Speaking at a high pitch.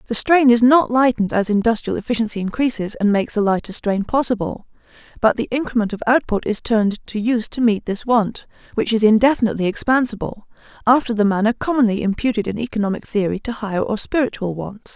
Yes: high, 225 Hz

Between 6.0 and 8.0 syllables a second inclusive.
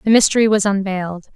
Yes: 6.5 syllables/s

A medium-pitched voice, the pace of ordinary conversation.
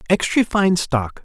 Yes: medium, 170 Hz; average, 145 wpm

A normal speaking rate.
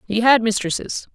Yes: average, 155 wpm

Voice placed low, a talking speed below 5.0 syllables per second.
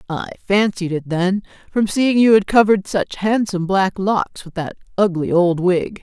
No: high, 195 Hz; 4.8 syllables/s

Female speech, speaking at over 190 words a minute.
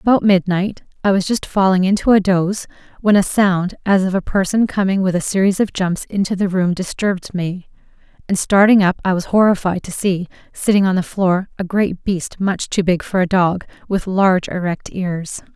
Yes: female; average, 200 wpm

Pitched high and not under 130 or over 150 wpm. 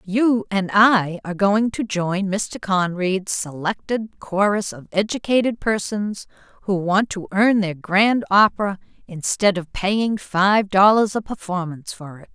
Yes: high, 200 Hz; average, 145 wpm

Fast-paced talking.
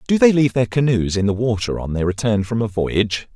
Yes: fast, 250 wpm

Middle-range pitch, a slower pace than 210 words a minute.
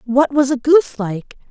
No: very high, 265 Hz; average, 200 wpm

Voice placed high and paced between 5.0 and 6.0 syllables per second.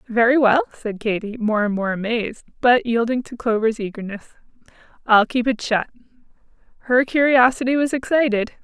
Yes: high, 235 Hz; 5.3 syllables/s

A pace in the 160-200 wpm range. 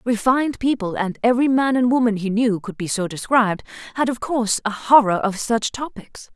Yes: average, 180 wpm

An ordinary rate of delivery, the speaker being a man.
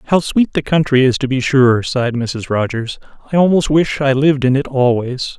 No: fast, 210 wpm; male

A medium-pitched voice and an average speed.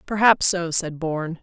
Yes: medium, 170 Hz; average, 170 wpm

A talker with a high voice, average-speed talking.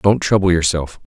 No: very low, 90 Hz; average, 150 wpm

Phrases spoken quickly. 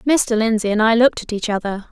Yes: fast, 250 wpm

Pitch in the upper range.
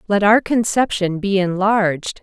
Yes: high, 200 Hz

